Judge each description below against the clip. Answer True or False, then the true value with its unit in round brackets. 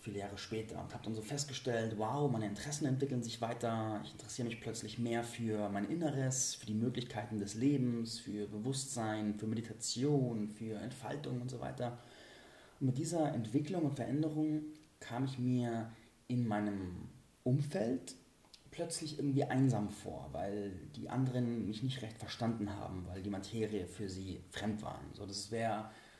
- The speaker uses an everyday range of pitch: True (3.6 semitones)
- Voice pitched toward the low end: True (115 Hz)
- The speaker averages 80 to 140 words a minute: False (160 wpm)